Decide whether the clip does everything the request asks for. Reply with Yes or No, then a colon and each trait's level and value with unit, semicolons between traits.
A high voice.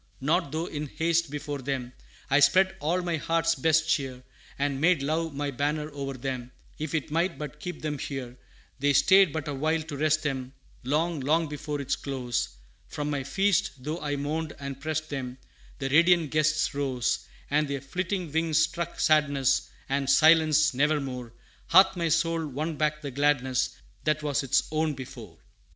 No: medium, 150 Hz